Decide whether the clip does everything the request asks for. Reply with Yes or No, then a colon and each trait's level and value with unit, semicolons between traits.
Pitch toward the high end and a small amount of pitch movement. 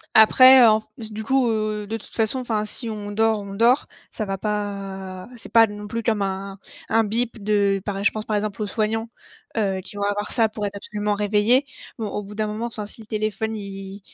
Yes: high, 210 Hz; narrow, 1.7 semitones